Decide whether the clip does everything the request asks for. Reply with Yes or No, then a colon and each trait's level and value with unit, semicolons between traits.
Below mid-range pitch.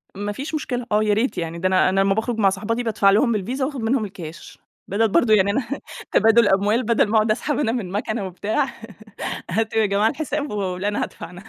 No: high, 215 Hz